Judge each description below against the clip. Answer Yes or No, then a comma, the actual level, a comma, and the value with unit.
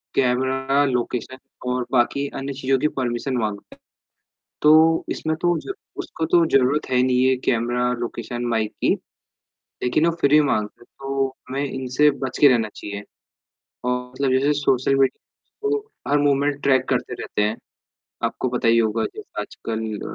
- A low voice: Yes, low, 130 Hz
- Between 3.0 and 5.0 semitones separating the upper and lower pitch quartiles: No, narrow, 2.6 semitones